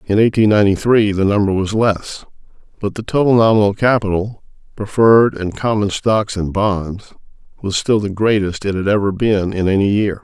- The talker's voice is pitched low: Yes, low, 105 Hz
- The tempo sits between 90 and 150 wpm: No, average, 175 wpm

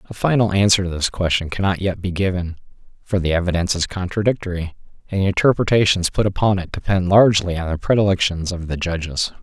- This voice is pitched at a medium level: No, very low, 95 Hz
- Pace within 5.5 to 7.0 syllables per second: Yes, 6.3 syllables/s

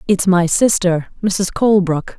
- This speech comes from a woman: Yes, female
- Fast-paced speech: No, slow, 135 wpm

